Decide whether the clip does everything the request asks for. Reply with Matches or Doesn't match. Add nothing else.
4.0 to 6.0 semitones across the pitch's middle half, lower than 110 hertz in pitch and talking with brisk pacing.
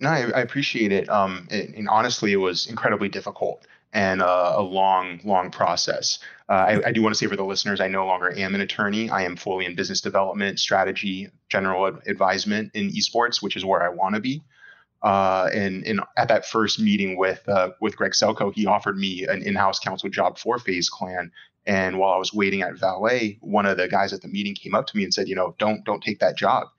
Doesn't match